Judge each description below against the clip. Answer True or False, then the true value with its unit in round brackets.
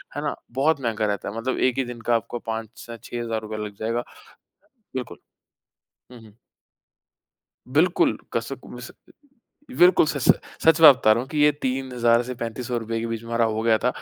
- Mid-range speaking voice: False (120 Hz)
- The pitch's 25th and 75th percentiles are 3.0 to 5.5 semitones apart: False (2.4 semitones)